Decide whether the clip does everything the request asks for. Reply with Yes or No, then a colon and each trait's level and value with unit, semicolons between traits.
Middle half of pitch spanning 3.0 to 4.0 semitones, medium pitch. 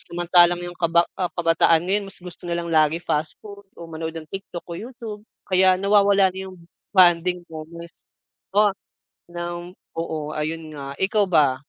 No: narrow, 2.5 semitones; medium, 175 Hz